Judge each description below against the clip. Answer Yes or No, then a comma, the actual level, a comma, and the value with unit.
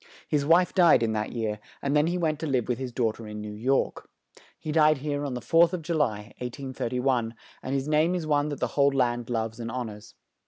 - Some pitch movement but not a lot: Yes, average, 4.7 semitones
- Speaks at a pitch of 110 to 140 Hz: Yes, low, 135 Hz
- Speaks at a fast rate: Yes, fast, 240 wpm